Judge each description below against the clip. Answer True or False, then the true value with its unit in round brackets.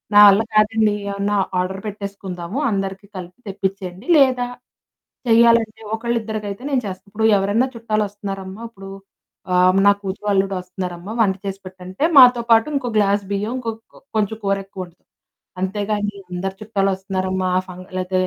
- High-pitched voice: True (200 Hz)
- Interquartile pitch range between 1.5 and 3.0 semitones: True (2.4 semitones)